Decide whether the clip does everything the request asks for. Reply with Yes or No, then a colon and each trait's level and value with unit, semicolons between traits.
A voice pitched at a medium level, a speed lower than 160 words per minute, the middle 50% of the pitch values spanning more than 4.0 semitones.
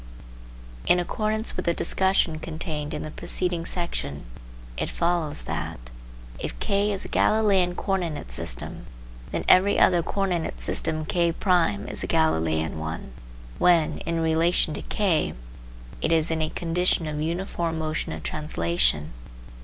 No: medium, 165 Hz; average, 145 wpm; average, 2.7 semitones